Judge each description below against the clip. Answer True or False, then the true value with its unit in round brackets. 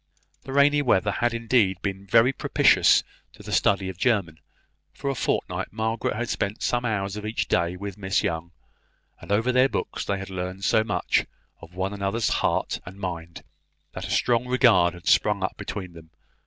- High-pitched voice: False (100 Hz)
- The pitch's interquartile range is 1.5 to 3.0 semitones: False (3.8 semitones)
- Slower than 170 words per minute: False (185 wpm)